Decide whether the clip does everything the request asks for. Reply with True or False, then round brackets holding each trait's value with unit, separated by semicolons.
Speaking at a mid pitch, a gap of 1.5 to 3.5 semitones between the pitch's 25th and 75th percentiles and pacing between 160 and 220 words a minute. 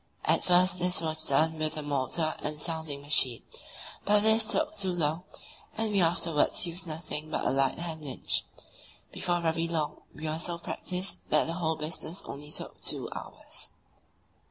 True (160 Hz; 2.7 semitones; 170 wpm)